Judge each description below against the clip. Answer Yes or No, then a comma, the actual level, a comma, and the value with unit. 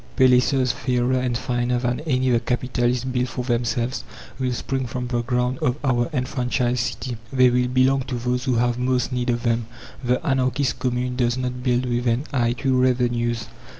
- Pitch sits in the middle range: No, low, 125 Hz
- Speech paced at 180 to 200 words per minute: Yes, average, 185 wpm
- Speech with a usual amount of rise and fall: No, narrow, 1.0 semitones